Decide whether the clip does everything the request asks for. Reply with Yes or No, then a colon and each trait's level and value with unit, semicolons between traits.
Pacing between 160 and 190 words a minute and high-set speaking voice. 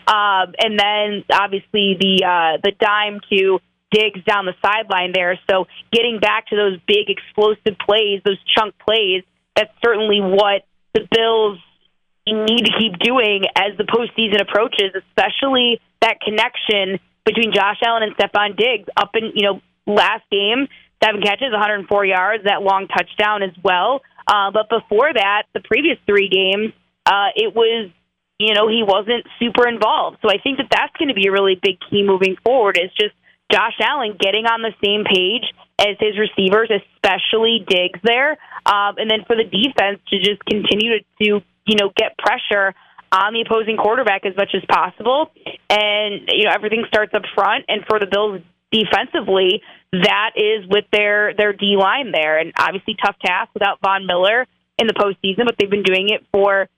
Yes: average, 180 wpm; high, 210 Hz